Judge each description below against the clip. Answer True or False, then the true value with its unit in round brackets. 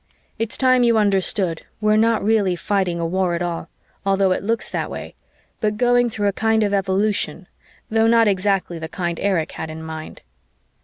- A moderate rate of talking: True (185 wpm)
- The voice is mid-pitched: False (200 Hz)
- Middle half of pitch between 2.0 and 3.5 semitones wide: False (3.9 semitones)